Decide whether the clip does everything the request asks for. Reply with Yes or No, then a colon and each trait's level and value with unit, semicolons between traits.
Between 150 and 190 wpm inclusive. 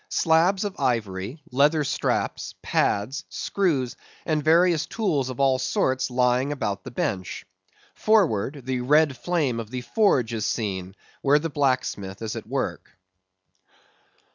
No: slow, 135 wpm